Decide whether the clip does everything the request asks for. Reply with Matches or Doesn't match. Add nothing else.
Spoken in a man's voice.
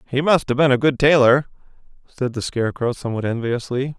Matches